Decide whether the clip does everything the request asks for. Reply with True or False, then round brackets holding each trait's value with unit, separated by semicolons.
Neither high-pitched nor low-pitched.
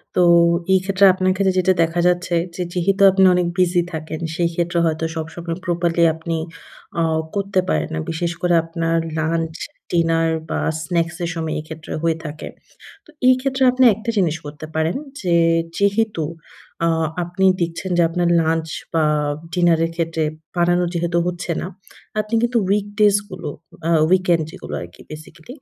True (170 Hz)